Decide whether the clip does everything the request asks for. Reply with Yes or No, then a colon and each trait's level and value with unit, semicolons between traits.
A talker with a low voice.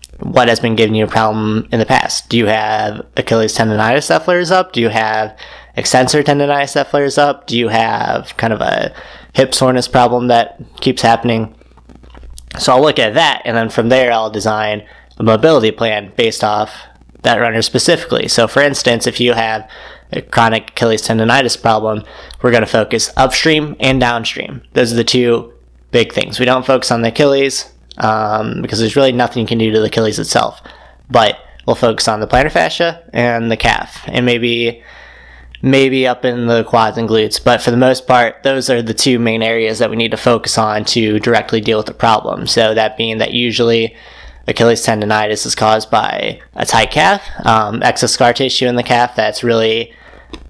Yes: low, 115 Hz